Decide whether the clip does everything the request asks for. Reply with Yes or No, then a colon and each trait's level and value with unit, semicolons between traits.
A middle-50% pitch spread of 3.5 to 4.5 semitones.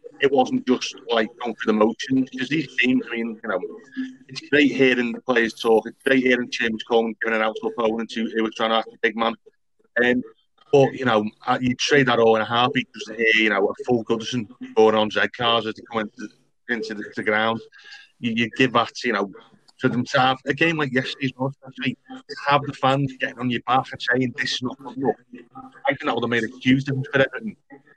No: average, 3.1 semitones